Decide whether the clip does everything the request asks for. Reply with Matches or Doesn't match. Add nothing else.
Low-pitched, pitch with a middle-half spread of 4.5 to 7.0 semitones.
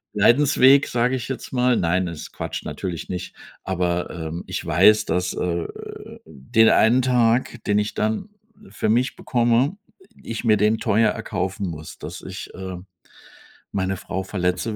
Matches